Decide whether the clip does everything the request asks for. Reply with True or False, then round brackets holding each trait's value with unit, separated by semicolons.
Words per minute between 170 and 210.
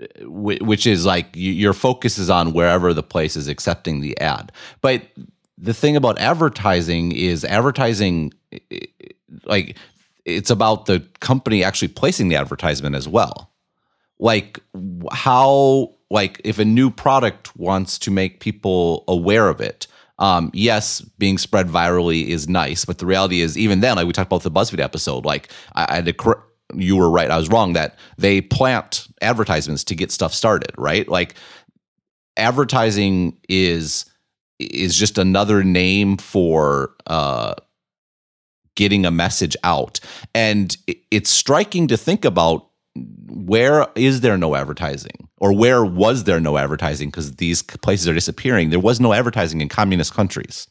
False (150 wpm)